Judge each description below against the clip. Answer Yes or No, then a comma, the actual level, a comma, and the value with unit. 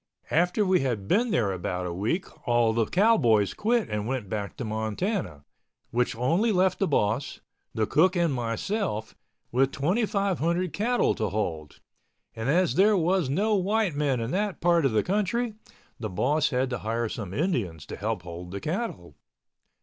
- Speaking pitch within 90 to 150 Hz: Yes, low, 135 Hz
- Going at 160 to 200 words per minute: Yes, average, 170 wpm